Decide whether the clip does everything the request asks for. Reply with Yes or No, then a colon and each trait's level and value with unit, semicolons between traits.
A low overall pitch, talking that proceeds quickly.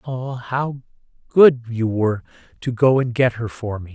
No: low, 120 Hz; average, 185 wpm